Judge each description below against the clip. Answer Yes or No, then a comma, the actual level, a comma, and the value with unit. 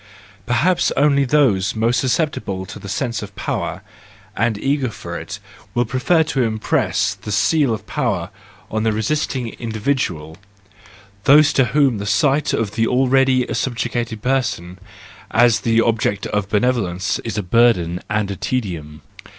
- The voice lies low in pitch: Yes, low, 115 Hz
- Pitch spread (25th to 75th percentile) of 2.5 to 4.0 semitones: No, average, 4.4 semitones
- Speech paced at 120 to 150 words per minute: Yes, average, 140 wpm